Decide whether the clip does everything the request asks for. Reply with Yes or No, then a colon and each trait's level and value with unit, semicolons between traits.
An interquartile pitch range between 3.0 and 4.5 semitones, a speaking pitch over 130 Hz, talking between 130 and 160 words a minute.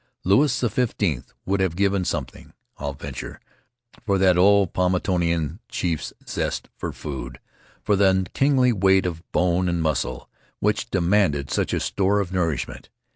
No: average, 3.4 semitones; very low, 90 Hz; average, 140 wpm